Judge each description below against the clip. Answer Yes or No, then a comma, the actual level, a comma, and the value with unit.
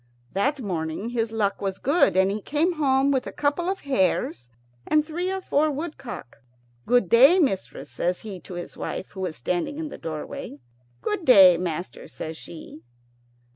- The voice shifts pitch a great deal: Yes, wide, 8.3 semitones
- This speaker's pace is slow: No, average, 175 wpm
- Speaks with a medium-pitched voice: No, high, 230 Hz